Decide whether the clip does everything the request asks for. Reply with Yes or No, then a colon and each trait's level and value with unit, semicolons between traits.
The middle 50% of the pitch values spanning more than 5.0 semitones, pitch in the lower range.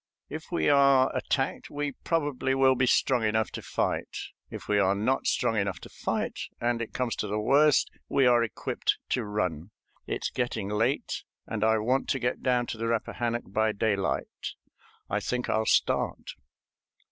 No: average, 3.7 semitones; low, 120 Hz